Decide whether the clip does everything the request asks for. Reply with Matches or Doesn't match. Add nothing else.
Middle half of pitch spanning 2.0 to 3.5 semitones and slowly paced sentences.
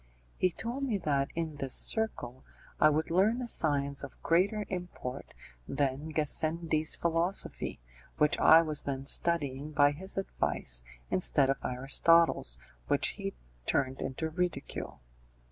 Doesn't match